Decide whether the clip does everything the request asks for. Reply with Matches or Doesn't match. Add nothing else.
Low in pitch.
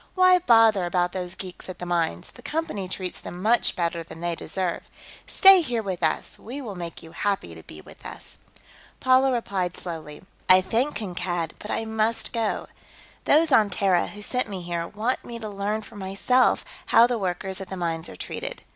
Doesn't match